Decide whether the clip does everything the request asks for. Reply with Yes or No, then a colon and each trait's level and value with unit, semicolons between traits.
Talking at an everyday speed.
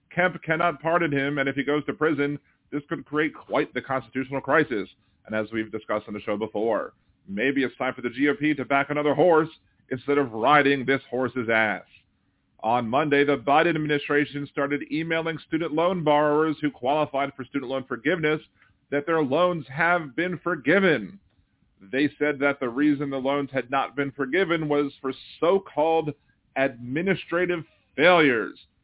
Yes: average, 165 wpm